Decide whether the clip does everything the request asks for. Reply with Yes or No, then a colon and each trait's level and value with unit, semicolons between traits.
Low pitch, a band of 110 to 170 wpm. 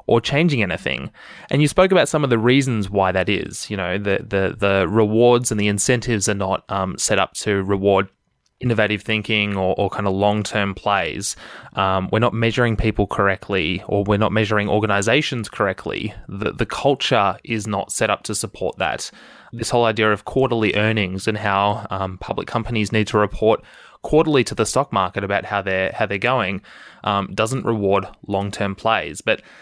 No: low, 105 Hz; average, 190 wpm